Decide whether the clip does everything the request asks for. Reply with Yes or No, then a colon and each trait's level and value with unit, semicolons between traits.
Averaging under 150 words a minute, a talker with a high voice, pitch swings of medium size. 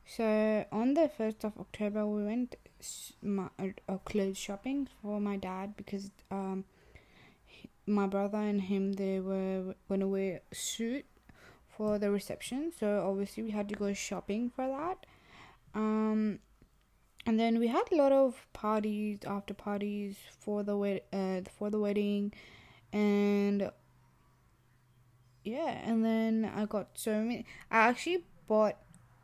No: average, 140 wpm; high, 205 Hz; narrow, 1.9 semitones